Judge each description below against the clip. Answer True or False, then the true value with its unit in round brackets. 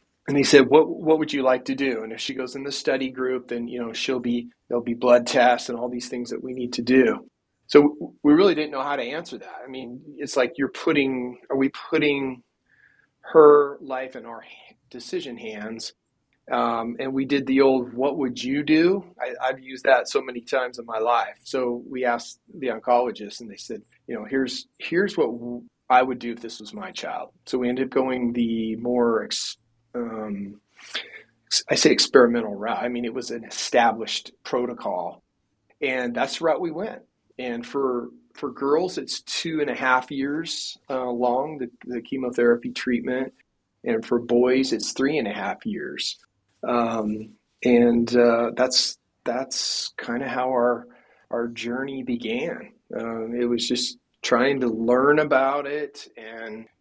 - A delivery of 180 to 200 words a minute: True (185 wpm)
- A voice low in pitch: True (125 Hz)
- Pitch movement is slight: True (2.1 semitones)